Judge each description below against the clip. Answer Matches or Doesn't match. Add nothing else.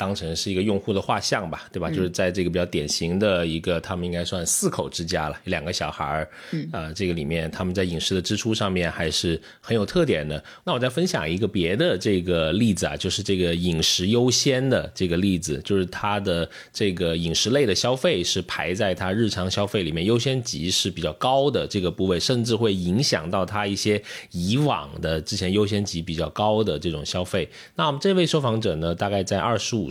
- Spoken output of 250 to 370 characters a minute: Matches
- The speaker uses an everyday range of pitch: Matches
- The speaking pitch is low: Matches